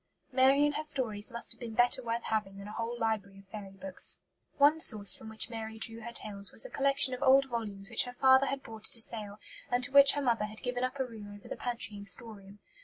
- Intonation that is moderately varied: Yes, average, 3.8 semitones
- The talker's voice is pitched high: Yes, high, 230 Hz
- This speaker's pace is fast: Yes, fast, 250 wpm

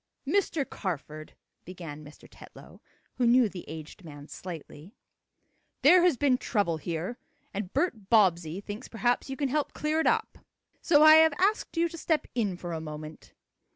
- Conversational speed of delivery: Yes, average, 165 wpm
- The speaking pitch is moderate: No, high, 210 Hz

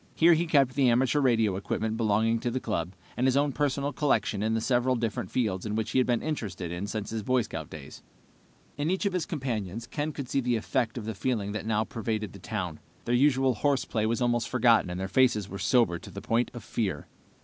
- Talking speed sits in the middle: No, fast, 225 wpm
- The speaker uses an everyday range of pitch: Yes, average, 3.4 semitones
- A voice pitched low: Yes, low, 115 Hz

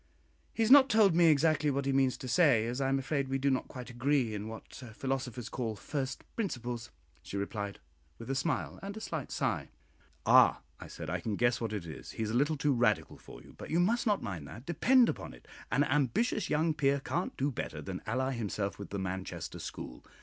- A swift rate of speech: Yes, fast, 220 wpm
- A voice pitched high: No, low, 135 Hz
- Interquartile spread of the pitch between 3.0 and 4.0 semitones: No, average, 5.2 semitones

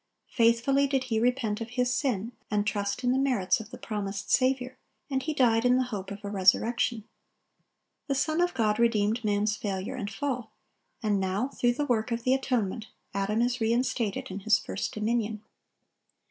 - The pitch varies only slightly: No, average, 3.5 semitones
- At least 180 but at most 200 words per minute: Yes, average, 185 wpm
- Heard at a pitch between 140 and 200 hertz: No, high, 230 Hz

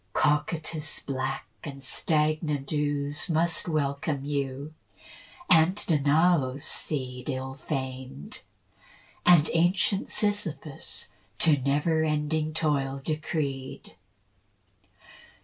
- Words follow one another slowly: Yes, slow, 80 wpm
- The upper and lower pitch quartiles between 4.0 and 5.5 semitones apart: No, narrow, 2.6 semitones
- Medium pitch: Yes, medium, 150 Hz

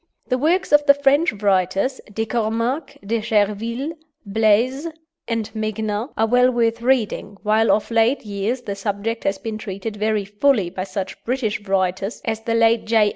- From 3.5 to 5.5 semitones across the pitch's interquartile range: No, average, 2.9 semitones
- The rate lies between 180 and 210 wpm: No, average, 165 wpm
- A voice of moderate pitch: No, high, 220 Hz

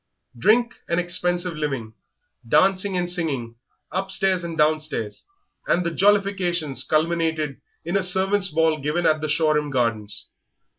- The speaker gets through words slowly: Yes, slow, 130 wpm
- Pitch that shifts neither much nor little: Yes, average, 3.6 semitones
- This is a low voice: No, medium, 165 Hz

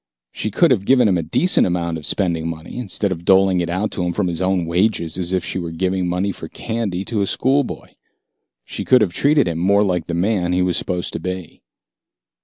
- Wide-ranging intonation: No, average, 2.9 semitones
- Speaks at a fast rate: Yes, fast, 225 wpm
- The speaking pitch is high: No, very low, 90 Hz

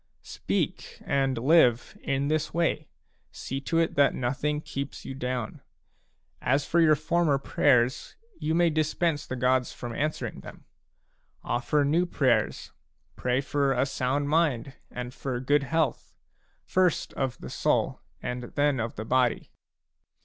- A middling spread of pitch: Yes, average, 3.4 semitones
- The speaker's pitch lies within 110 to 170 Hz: Yes, medium, 140 Hz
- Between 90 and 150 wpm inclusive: Yes, slow, 135 wpm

